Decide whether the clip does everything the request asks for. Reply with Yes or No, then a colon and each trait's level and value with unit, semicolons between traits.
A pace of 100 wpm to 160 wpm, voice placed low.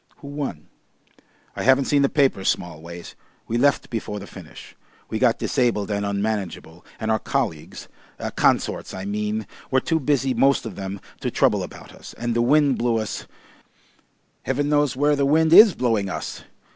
No: average, 170 wpm; low, 120 Hz